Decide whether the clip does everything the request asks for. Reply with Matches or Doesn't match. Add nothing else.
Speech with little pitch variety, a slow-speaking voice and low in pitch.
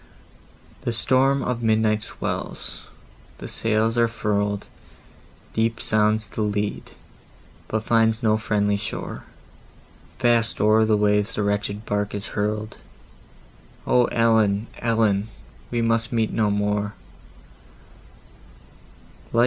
Matches